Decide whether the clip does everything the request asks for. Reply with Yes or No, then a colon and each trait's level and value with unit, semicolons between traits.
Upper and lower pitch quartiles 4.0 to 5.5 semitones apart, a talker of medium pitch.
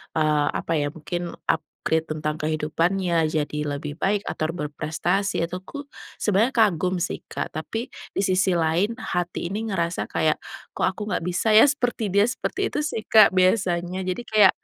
Yes: average, 4.5 semitones; medium, 180 Hz